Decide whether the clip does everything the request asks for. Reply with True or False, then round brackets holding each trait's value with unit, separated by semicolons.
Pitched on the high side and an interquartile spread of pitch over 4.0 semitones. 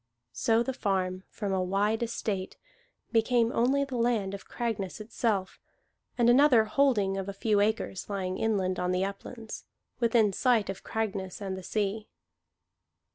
False (210 Hz; 3.2 semitones)